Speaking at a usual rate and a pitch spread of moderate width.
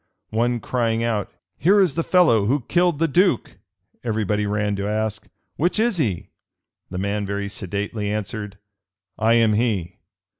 Yes: average, 155 wpm; average, 4.7 semitones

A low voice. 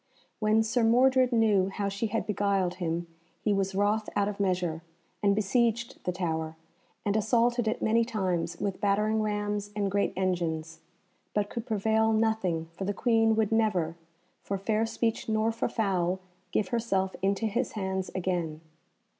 No: high, 205 Hz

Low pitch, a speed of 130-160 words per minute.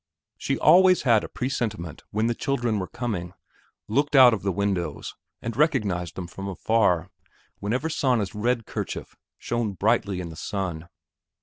Yes: low, 105 Hz; average, 150 wpm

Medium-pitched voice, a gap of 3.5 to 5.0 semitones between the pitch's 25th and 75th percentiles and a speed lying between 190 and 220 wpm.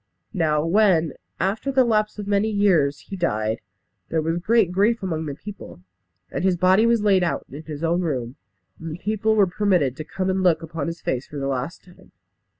Yes: medium, 175 Hz; average, 4.7 semitones; fast, 205 wpm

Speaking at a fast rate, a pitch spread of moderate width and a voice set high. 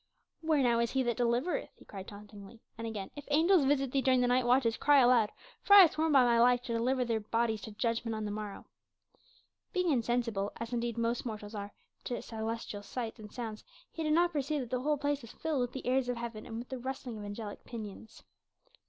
Yes: fast, 225 wpm; average, 3.1 semitones; high, 240 Hz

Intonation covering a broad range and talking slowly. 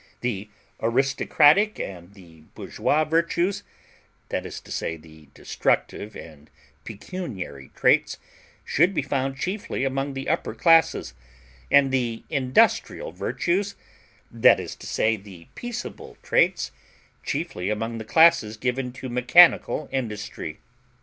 Yes: wide, 7.6 semitones; slow, 120 wpm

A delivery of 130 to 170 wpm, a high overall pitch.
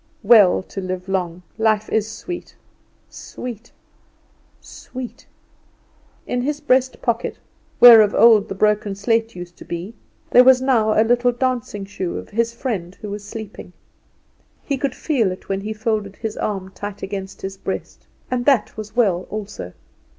Yes: average, 160 wpm; high, 215 Hz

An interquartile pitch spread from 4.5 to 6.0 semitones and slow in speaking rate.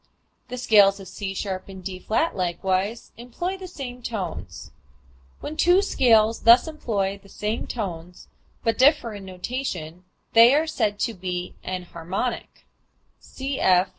Yes: average, 5.1 semitones; slow, 130 wpm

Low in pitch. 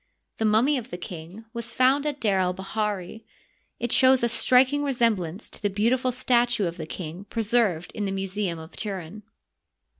No: high, 215 Hz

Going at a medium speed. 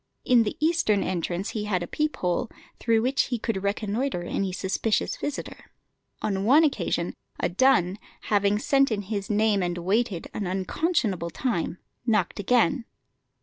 Yes: average, 150 wpm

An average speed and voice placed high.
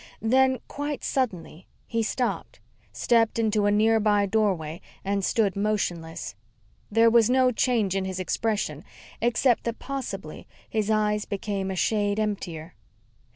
No: slow, 130 wpm; high, 215 Hz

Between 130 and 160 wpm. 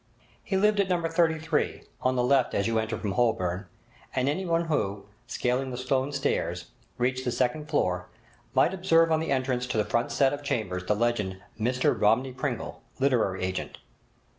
No: average, 175 wpm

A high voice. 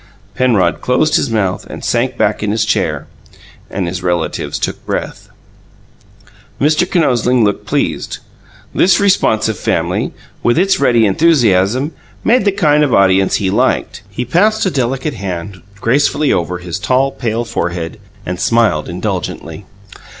No: low, 115 Hz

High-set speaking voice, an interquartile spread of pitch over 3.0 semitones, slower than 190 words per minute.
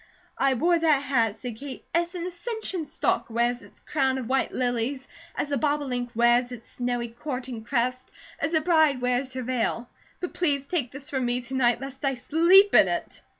No: very high, 265 Hz; average, 3.6 semitones; average, 195 wpm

